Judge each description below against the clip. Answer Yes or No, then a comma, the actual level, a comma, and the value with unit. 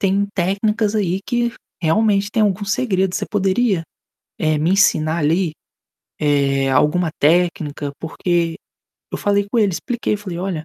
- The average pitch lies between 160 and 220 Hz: Yes, medium, 185 Hz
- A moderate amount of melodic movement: Yes, average, 4.0 semitones